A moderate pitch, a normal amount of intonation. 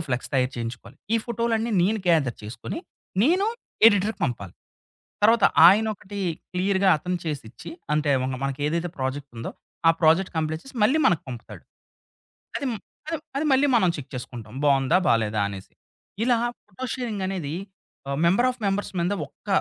No: medium, 170 Hz; wide, 8.4 semitones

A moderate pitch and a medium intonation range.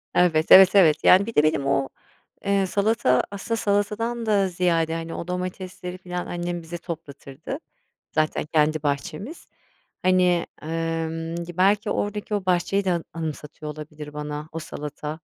Yes: medium, 170 Hz; average, 3.6 semitones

